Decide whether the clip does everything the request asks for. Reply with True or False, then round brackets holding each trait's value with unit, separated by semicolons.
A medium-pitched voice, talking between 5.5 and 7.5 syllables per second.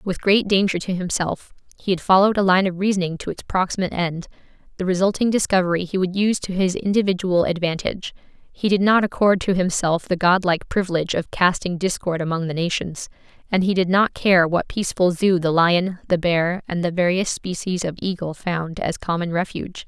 True (180 Hz; 5.7 syllables/s)